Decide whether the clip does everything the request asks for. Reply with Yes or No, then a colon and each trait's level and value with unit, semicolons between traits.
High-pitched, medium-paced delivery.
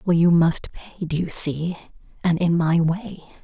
No: medium, 170 Hz; average, 190 wpm